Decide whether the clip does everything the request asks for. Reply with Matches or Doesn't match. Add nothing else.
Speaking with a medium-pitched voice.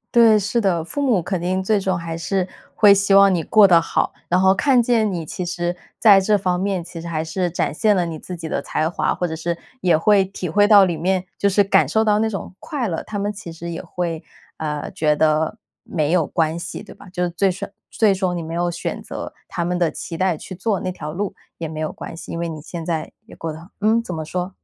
Matches